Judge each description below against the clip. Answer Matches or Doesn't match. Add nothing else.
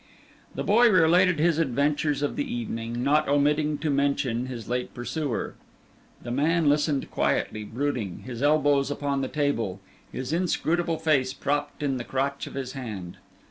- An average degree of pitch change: Matches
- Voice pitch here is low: Doesn't match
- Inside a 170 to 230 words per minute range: Doesn't match